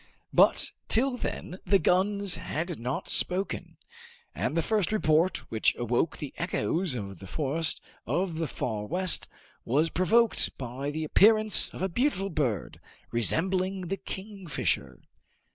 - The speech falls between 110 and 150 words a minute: Yes, slow, 135 wpm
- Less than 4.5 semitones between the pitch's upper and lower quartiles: No, average, 5.2 semitones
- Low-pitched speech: No, medium, 175 Hz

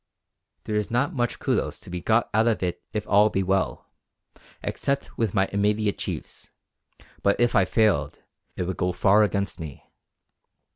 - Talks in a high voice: No, low, 105 Hz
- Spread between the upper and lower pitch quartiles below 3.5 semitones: Yes, average, 2.7 semitones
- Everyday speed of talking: Yes, average, 165 wpm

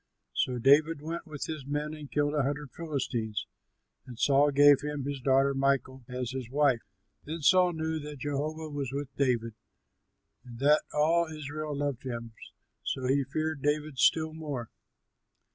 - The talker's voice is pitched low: No, medium, 145 Hz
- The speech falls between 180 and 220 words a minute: No, average, 160 wpm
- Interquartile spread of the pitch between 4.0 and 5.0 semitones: No, narrow, 2.5 semitones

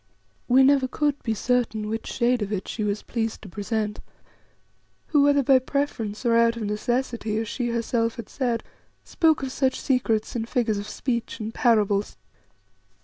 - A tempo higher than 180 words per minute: No, average, 165 wpm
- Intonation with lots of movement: No, average, 3.2 semitones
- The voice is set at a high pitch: Yes, high, 230 Hz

